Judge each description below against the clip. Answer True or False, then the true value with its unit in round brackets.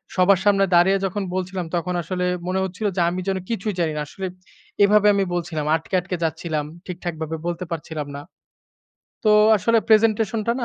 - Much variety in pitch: False (3.0 semitones)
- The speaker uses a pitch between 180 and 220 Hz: True (185 Hz)